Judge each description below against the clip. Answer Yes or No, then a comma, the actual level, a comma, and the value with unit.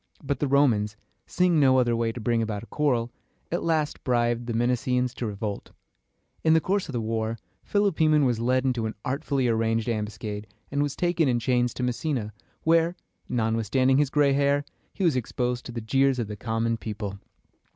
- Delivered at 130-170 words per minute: No, average, 185 wpm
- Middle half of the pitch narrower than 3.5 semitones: No, average, 3.9 semitones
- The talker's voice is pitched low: Yes, low, 125 Hz